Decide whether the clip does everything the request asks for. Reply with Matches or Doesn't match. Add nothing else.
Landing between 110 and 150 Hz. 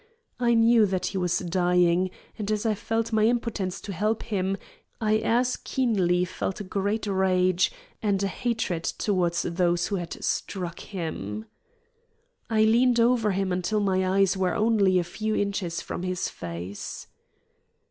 Doesn't match